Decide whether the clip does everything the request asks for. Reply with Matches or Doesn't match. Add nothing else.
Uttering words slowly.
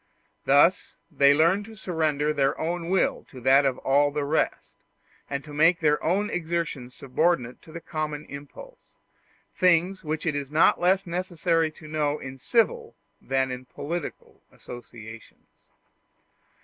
Doesn't match